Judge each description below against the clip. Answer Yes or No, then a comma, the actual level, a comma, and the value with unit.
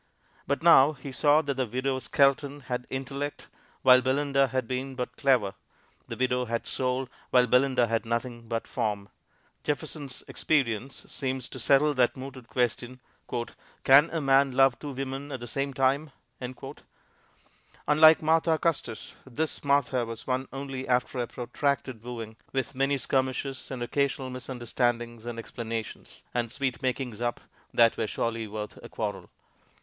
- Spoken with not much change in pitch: Yes, narrow, 2.3 semitones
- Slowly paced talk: No, average, 150 wpm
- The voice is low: Yes, low, 130 Hz